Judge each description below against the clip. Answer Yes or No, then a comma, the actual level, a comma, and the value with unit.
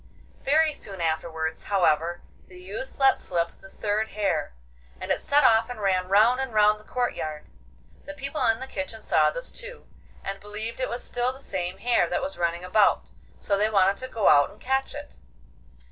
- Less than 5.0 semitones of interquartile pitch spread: No, wide, 5.5 semitones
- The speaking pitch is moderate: No, high, 210 Hz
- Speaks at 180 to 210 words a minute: Yes, average, 195 wpm